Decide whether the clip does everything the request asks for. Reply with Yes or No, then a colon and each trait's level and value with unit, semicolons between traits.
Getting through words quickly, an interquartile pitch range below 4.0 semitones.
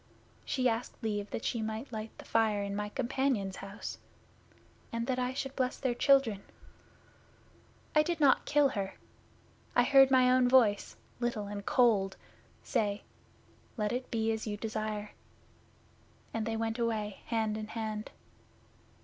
No: average, 150 wpm; average, 3.2 semitones